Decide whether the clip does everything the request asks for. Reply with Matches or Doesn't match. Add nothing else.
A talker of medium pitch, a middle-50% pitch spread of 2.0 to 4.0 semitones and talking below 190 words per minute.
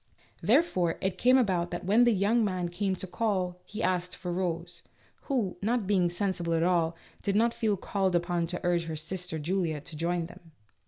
Doesn't match